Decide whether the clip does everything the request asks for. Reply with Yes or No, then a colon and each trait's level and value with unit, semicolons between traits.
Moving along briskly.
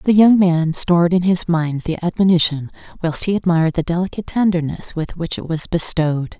No: average, 190 wpm